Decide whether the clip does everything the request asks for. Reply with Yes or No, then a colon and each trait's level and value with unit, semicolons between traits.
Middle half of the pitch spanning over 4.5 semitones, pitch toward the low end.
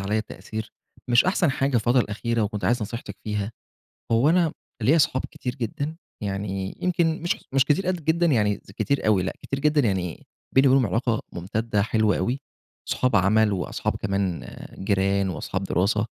Yes: wide, 5.4 semitones; low, 110 Hz